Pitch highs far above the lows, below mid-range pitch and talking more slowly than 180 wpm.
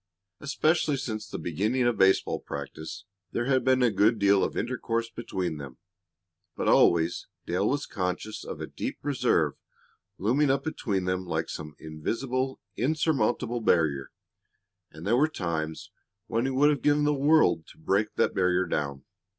Yes: wide, 7.0 semitones; low, 110 Hz; average, 160 wpm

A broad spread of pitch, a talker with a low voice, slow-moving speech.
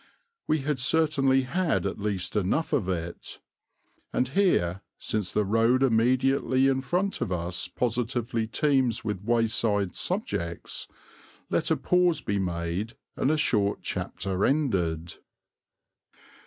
Yes: wide, 5.7 semitones; low, 115 Hz; slow, 125 wpm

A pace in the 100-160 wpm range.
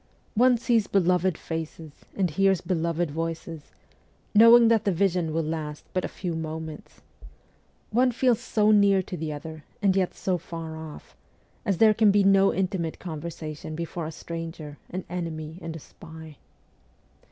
Yes: average, 155 wpm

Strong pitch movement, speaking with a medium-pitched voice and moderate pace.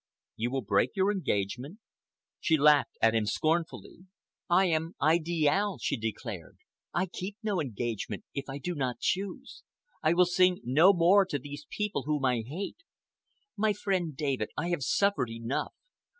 Yes: wide, 6.2 semitones; medium, 155 Hz; average, 155 wpm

